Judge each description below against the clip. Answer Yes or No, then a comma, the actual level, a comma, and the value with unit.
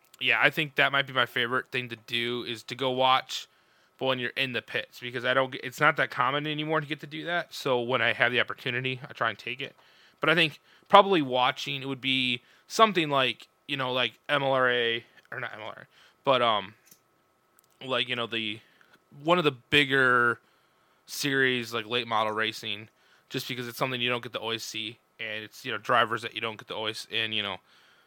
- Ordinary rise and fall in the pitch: Yes, average, 3.0 semitones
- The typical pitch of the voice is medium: No, low, 130 Hz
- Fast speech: Yes, fast, 215 wpm